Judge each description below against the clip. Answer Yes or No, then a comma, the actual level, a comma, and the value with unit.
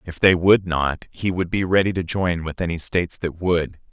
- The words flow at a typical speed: No, fast, 230 wpm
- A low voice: Yes, very low, 85 Hz